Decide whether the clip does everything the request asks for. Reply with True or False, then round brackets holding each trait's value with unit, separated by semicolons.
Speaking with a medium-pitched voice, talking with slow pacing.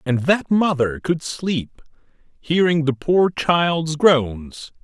True (155 Hz; 125 wpm)